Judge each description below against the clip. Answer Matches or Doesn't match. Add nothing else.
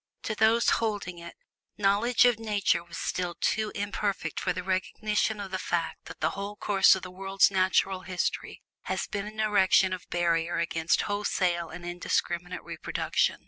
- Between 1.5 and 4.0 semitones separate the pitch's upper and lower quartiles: Matches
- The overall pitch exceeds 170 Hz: Matches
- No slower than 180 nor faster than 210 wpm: Doesn't match